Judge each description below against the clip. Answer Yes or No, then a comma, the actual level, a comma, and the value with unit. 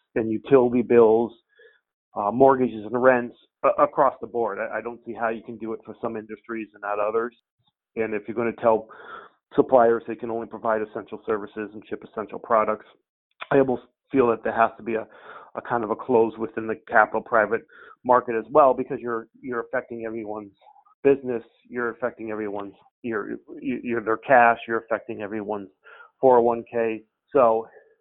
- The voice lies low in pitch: Yes, low, 115 Hz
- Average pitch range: No, narrow, 1.7 semitones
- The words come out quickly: No, average, 175 wpm